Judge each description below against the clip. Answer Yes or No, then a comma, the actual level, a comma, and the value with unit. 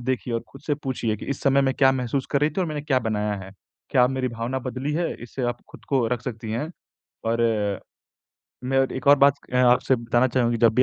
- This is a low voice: Yes, low, 125 Hz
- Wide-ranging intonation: No, narrow, 2.6 semitones